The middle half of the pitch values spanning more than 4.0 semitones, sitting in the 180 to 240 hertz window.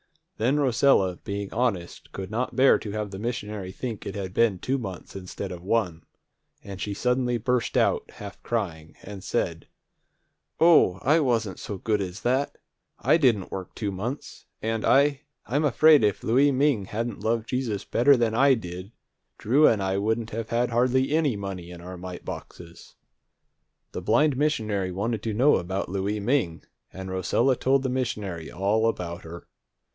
No: average, 4.9 semitones; low, 110 Hz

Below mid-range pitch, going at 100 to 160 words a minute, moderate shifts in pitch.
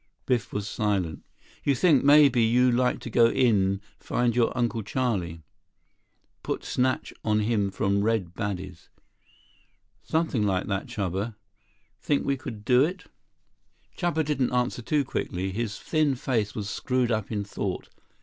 Yes: low, 115 Hz; average, 150 wpm; average, 4.2 semitones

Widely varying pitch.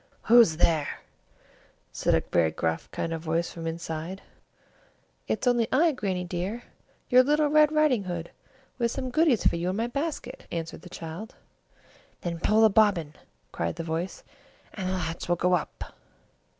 Yes: wide, 6.6 semitones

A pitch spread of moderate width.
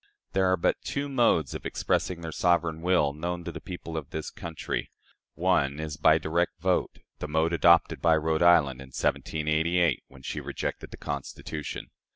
No: narrow, 2.2 semitones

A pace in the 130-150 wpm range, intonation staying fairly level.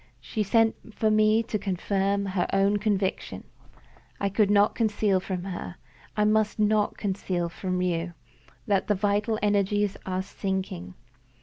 Yes: average, 140 wpm; narrow, 2.1 semitones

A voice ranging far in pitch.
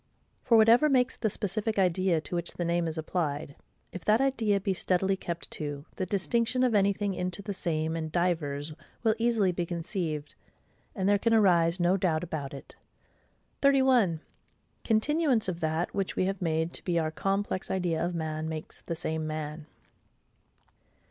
No: average, 4.3 semitones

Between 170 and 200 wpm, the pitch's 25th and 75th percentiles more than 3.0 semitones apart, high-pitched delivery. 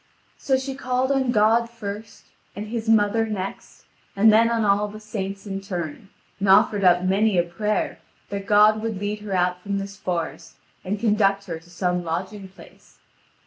No: average, 180 wpm; narrow, 2.4 semitones; high, 205 Hz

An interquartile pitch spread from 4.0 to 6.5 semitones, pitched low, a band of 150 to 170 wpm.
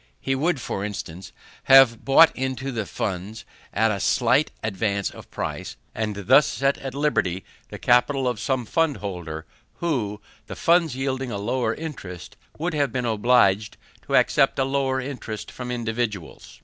Yes: average, 4.5 semitones; low, 125 Hz; average, 155 wpm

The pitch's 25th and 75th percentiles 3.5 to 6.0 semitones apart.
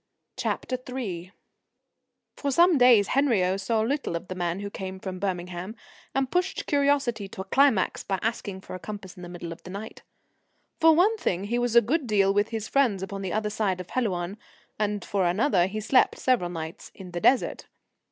Yes: average, 5.3 semitones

